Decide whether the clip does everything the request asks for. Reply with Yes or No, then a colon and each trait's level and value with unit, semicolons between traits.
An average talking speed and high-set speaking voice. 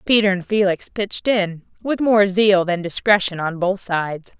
Yes: average, 180 wpm; high, 195 Hz